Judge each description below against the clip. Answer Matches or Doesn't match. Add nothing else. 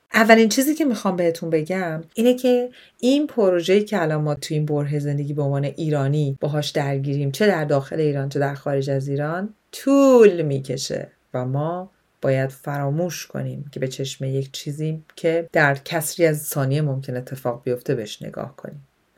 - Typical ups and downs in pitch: Matches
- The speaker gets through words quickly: Matches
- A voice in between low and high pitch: Matches